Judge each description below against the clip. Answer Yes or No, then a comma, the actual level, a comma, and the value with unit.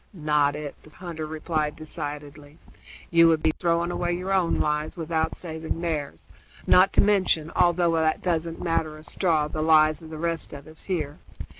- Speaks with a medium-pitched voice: Yes, medium, 160 Hz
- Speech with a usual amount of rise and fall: No, narrow, 1.9 semitones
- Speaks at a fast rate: No, average, 175 wpm